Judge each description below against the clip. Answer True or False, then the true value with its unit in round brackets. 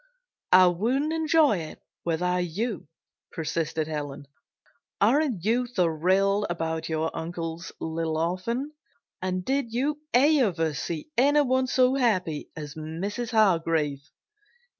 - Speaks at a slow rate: True (110 wpm)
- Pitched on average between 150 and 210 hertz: True (185 Hz)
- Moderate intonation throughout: False (7.3 semitones)